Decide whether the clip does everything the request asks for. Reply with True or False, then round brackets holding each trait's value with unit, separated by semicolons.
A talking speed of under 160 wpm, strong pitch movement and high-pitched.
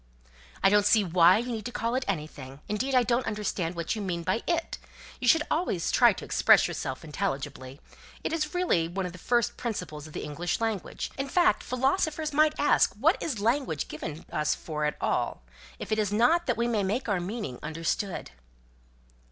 False (195 wpm; 7.1 semitones; 210 Hz)